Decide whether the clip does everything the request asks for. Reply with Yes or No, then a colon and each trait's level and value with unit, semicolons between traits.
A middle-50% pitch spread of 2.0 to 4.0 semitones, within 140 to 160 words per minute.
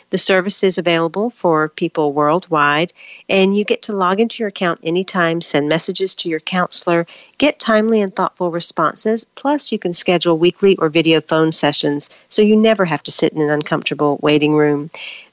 No: average, 3.7 semitones; average, 180 wpm